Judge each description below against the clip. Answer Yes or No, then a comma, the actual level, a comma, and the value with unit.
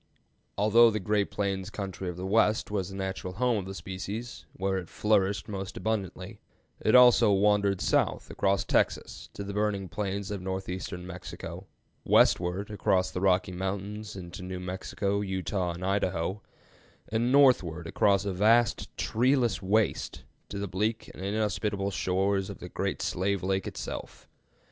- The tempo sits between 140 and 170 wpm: Yes, average, 155 wpm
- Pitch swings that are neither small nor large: No, narrow, 2.0 semitones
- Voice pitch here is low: Yes, low, 100 Hz